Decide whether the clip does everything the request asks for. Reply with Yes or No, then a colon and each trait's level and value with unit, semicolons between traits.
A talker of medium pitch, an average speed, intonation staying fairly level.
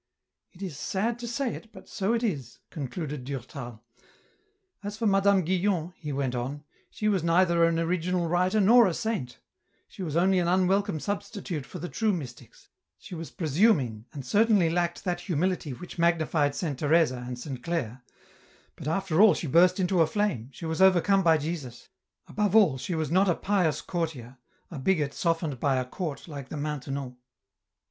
No: medium, 170 Hz; average, 185 wpm; average, 5.1 semitones